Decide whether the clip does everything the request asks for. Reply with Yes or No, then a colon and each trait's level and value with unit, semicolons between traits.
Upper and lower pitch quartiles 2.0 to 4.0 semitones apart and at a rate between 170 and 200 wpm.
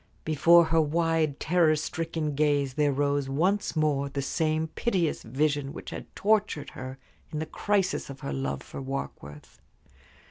No: average, 2.8 semitones; average, 150 wpm